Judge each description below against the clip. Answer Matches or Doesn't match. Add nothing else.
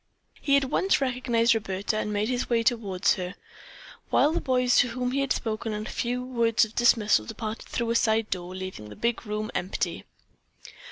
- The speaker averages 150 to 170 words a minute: Doesn't match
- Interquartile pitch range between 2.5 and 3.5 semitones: Matches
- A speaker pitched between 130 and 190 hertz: Doesn't match